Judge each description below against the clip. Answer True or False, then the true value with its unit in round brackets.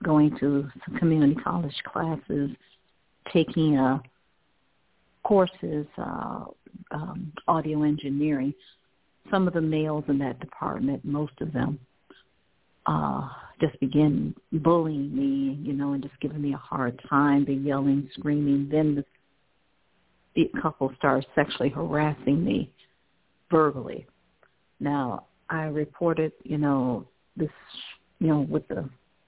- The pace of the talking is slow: True (120 wpm)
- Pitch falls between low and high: True (145 Hz)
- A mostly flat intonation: True (2.1 semitones)